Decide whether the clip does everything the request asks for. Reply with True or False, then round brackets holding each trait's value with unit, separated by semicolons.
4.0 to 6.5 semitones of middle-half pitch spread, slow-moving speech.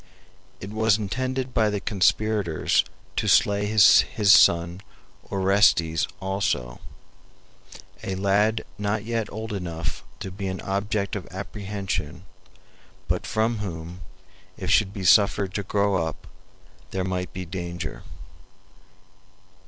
False (2.5 semitones; 120 wpm)